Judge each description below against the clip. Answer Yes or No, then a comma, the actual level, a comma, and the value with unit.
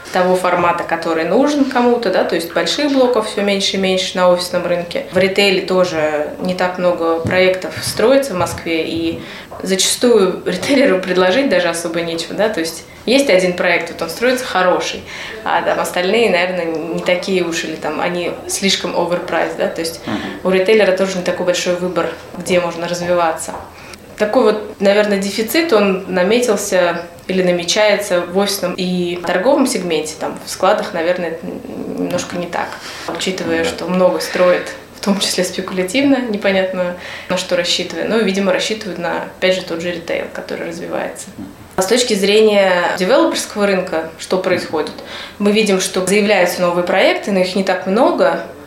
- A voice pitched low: No, medium, 185 Hz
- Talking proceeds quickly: Yes, fast, 165 wpm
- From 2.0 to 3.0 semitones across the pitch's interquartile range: Yes, narrow, 2.6 semitones